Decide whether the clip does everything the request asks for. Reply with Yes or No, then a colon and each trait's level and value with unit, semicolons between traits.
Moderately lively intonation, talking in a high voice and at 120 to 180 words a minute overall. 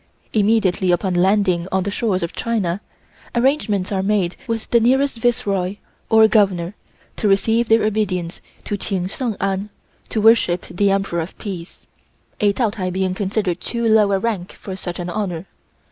Yes: average, 3.2 semitones; high, 200 Hz; average, 165 wpm